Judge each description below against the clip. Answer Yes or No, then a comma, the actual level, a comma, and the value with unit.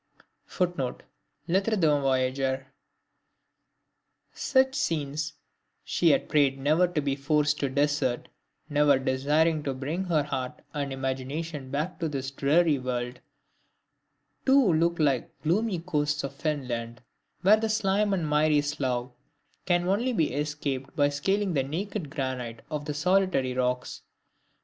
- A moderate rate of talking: No, slow, 130 wpm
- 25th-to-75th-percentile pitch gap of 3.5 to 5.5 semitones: Yes, average, 4.1 semitones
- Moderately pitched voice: Yes, medium, 150 Hz